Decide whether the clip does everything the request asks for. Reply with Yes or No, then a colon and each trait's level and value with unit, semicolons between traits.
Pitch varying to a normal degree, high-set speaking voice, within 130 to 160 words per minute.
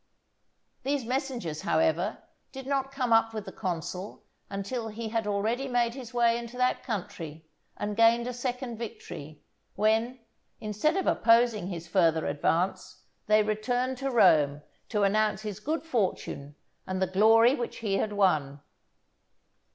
Yes: average, 4.5 semitones; high, 220 Hz; average, 145 wpm